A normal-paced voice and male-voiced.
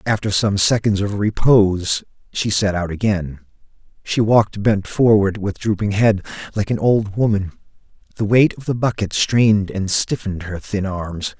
Yes: average, 165 wpm; male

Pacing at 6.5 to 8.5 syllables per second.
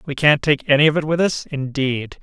No: 5.3 syllables/s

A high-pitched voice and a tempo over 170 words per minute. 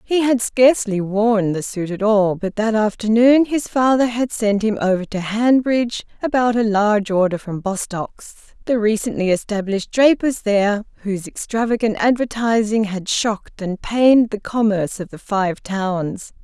No: high, 215 Hz; average, 155 wpm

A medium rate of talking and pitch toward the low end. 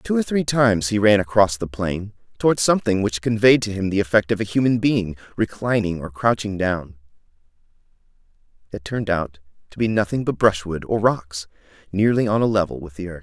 Yes: average, 190 wpm; low, 100 Hz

